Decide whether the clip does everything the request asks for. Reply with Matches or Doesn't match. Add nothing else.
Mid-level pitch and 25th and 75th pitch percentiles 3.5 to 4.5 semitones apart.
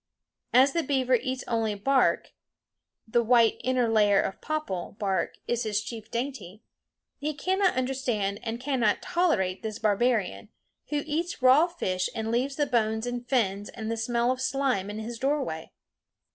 Doesn't match